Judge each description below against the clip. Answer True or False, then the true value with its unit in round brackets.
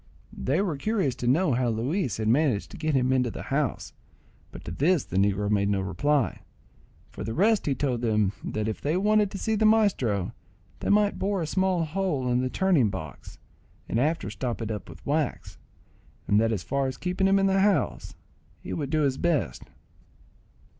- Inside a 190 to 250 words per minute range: True (195 wpm)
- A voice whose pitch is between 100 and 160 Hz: True (140 Hz)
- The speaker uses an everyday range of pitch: False (8.7 semitones)